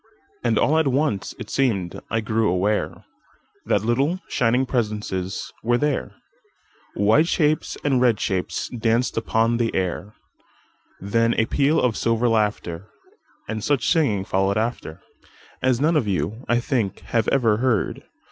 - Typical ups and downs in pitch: Yes, average, 3.7 semitones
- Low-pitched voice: Yes, low, 115 Hz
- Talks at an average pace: No, slow, 130 wpm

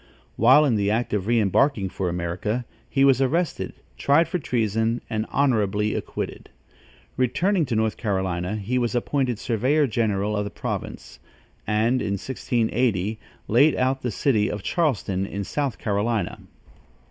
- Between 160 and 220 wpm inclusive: No, average, 145 wpm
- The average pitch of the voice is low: Yes, low, 115 Hz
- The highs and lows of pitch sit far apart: No, average, 4.2 semitones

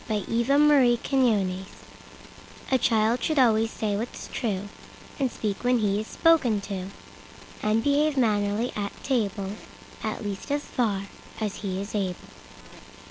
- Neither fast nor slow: No, slow, 130 wpm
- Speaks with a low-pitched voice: No, high, 220 Hz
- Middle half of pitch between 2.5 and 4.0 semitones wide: Yes, average, 3.7 semitones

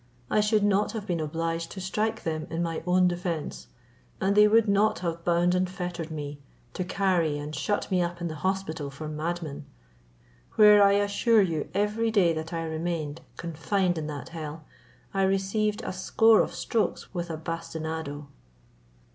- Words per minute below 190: Yes, average, 170 wpm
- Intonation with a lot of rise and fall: No, average, 3.8 semitones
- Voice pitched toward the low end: No, medium, 175 Hz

